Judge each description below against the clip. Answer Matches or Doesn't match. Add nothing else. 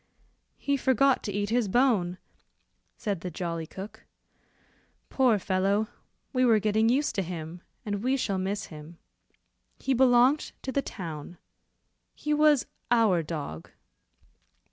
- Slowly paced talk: Matches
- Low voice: Doesn't match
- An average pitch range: Doesn't match